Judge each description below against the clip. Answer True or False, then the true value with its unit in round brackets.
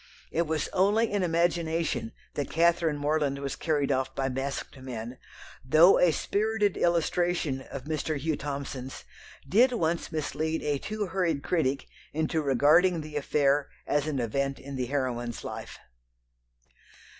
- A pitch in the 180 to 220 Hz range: False (150 Hz)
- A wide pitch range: False (3.7 semitones)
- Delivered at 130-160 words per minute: True (140 wpm)